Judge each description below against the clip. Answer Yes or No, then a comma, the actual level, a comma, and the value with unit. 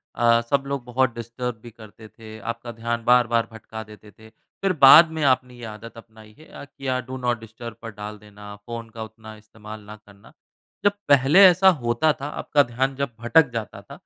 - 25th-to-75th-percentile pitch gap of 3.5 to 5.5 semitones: No, average, 3.0 semitones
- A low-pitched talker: Yes, low, 115 Hz